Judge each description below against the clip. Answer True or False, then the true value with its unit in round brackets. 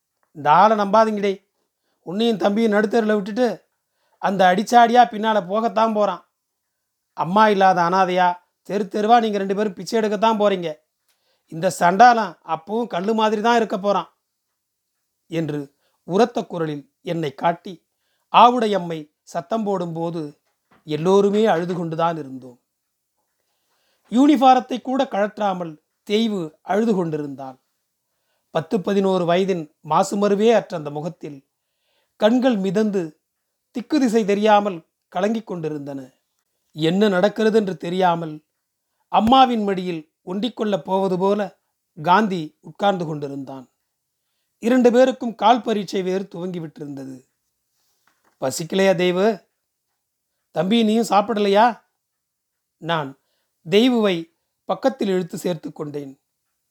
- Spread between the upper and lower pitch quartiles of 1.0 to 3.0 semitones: False (4.7 semitones)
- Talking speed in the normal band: True (100 wpm)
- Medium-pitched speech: False (195 Hz)